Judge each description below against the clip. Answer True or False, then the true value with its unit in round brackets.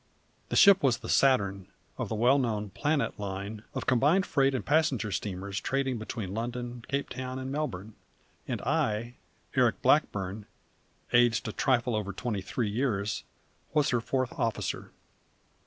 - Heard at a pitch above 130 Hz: False (120 Hz)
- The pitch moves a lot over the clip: False (4.3 semitones)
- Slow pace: False (150 wpm)